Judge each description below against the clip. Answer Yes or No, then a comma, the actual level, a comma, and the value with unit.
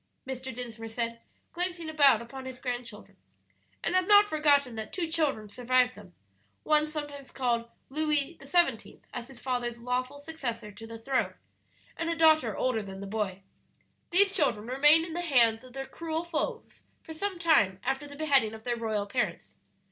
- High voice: Yes, very high, 260 Hz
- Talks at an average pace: Yes, average, 170 wpm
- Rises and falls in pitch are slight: No, average, 5.2 semitones